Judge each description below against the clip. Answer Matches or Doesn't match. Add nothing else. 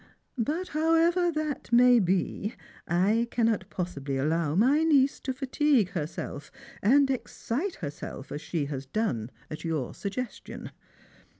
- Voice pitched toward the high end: Matches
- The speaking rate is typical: Doesn't match